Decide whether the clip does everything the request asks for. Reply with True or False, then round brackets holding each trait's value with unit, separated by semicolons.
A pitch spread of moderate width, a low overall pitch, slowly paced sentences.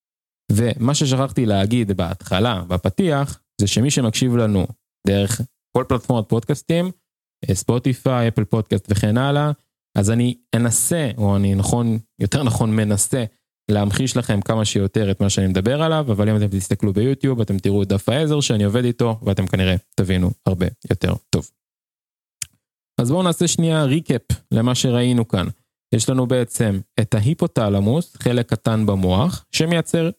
False (4.5 semitones; 115 Hz; 140 wpm)